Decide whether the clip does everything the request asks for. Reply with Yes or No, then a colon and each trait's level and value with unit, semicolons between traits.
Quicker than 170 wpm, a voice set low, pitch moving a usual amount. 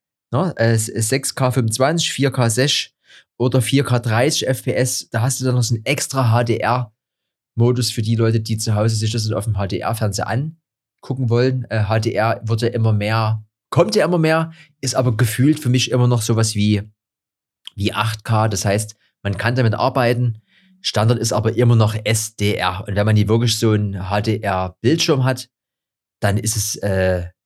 Yes: average, 180 wpm; low, 115 Hz; average, 3.0 semitones